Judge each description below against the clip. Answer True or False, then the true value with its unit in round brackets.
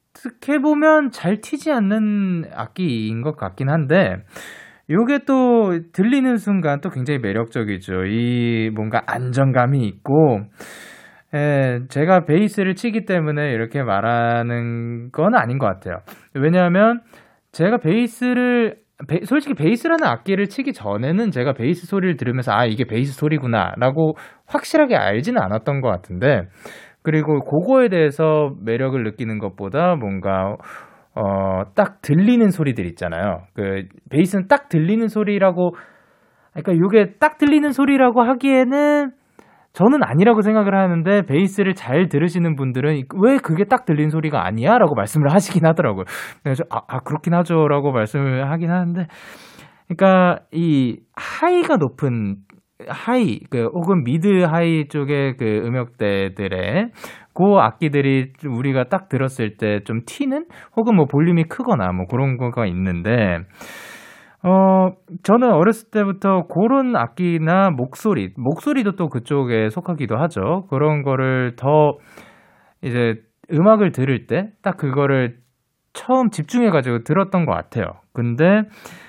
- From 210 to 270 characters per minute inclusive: False (300 characters per minute)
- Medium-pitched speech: True (160 Hz)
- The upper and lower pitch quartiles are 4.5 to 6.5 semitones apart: False (8.2 semitones)